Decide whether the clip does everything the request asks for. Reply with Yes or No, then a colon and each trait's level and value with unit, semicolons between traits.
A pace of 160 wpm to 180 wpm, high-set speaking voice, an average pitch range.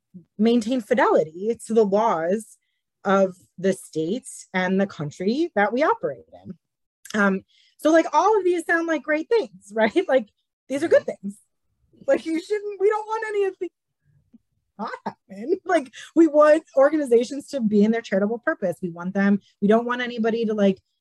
No: average, 175 wpm; high, 235 Hz; wide, 8.7 semitones